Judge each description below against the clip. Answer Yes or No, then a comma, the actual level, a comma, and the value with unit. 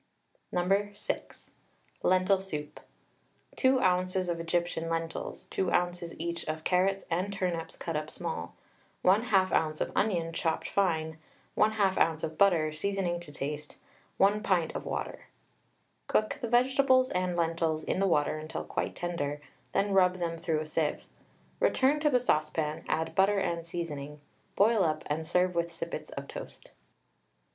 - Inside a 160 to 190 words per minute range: No, average, 150 wpm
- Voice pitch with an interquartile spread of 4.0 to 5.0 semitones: No, average, 3.4 semitones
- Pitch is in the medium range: Yes, medium, 175 Hz